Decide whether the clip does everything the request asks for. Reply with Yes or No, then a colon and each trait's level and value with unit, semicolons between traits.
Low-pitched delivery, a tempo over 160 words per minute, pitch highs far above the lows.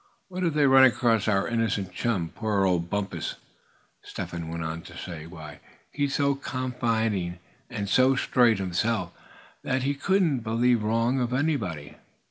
No: low, 115 Hz; average, 155 wpm; wide, 6.0 semitones